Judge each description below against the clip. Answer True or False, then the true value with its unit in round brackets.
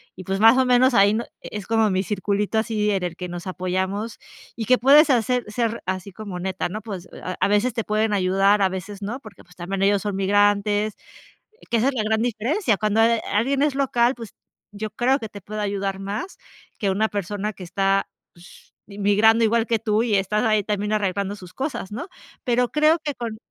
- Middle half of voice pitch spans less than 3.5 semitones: True (2.8 semitones)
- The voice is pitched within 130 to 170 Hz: False (210 Hz)